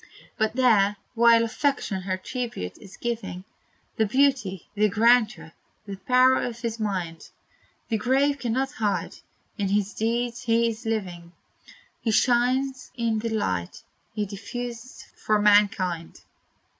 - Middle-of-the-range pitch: No, high, 225 Hz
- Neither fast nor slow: No, slow, 130 wpm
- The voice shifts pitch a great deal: No, average, 3.5 semitones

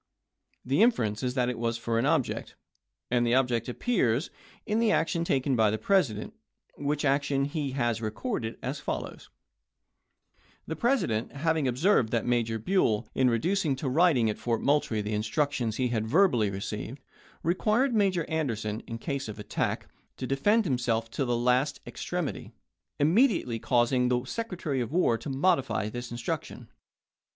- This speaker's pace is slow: No, average, 160 wpm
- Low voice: Yes, low, 130 Hz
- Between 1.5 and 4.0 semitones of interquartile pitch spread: No, wide, 5.5 semitones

